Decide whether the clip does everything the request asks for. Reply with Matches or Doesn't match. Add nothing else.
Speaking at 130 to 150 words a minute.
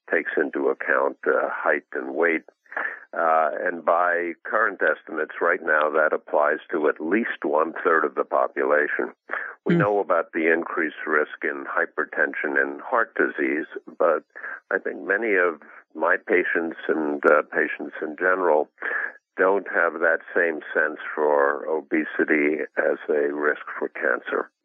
Matches